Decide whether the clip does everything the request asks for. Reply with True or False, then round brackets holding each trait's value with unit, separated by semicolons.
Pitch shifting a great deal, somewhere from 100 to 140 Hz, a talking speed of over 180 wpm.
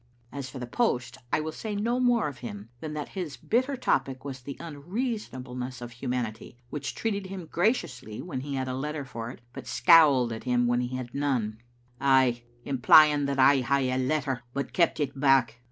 False (3.9 semitones; 135 Hz; 200 wpm)